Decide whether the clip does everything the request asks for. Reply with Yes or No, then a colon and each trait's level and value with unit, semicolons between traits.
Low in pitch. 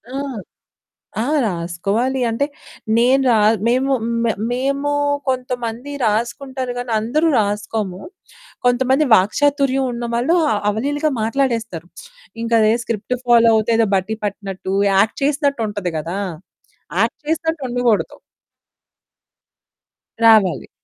No: high, 235 Hz